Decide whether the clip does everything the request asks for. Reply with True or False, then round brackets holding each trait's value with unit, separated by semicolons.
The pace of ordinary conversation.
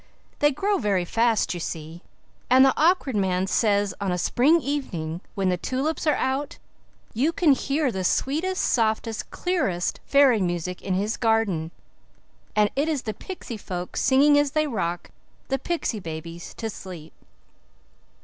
True (155 wpm)